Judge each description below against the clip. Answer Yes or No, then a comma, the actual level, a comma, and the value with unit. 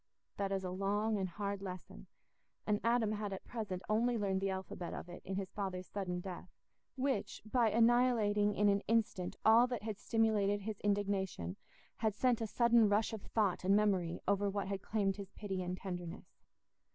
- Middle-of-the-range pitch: No, high, 205 Hz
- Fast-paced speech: No, average, 185 wpm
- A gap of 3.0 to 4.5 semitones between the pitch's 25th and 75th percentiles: No, narrow, 2.4 semitones